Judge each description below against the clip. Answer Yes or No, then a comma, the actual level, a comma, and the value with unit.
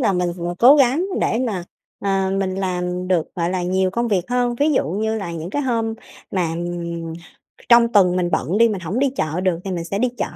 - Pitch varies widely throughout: No, average, 4.7 semitones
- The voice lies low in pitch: No, high, 190 Hz